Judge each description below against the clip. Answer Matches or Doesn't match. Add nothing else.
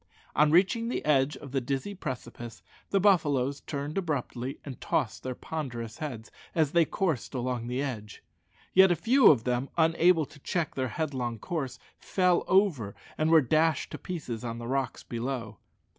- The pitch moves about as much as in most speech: Matches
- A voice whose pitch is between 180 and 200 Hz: Doesn't match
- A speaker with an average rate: Matches